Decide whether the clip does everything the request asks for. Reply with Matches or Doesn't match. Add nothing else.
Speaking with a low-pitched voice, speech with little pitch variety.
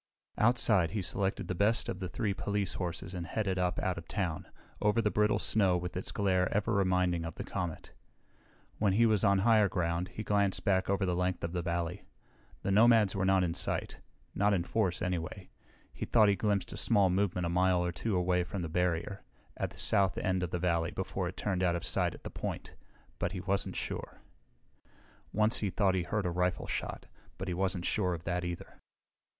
Matches